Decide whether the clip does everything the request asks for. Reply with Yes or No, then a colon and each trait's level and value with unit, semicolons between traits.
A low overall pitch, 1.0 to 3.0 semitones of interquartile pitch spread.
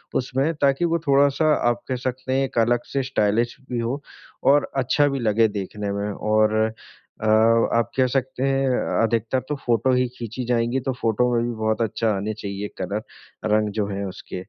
No: low, 120 Hz; average, 3.5 semitones